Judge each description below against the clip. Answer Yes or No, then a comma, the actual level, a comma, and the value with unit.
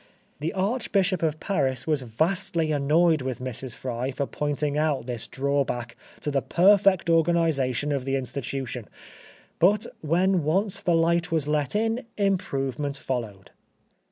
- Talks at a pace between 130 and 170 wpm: Yes, slow, 135 wpm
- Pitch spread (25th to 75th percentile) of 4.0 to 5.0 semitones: Yes, average, 4.6 semitones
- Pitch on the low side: No, medium, 150 Hz